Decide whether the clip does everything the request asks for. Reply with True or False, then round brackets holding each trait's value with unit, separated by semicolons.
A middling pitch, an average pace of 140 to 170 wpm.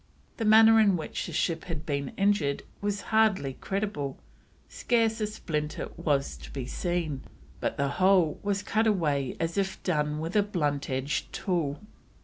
True (170 Hz; 160 wpm)